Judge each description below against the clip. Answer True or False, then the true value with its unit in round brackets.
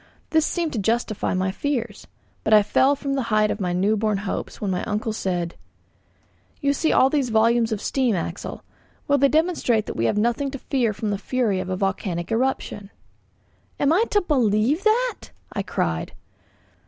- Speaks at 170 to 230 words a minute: True (185 wpm)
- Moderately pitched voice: False (225 Hz)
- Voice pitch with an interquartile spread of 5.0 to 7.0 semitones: True (5.6 semitones)